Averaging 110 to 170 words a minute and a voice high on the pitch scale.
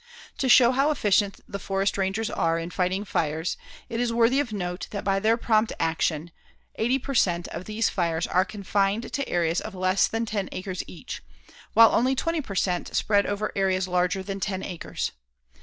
No: average, 190 wpm; high, 195 Hz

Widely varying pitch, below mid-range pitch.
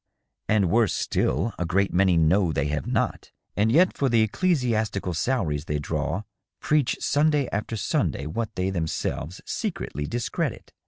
Yes: wide, 6.1 semitones; low, 100 Hz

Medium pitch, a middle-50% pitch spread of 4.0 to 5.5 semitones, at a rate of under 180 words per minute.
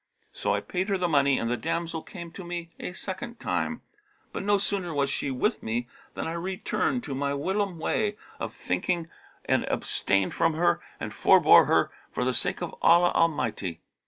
No: medium, 170 Hz; average, 4.9 semitones; average, 190 wpm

